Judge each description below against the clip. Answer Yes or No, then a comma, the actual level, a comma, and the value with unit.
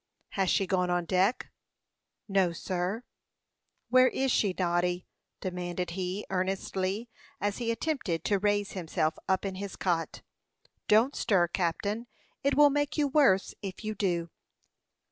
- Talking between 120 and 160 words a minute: Yes, average, 140 wpm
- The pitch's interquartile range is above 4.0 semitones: No, average, 3.4 semitones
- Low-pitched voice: No, high, 190 Hz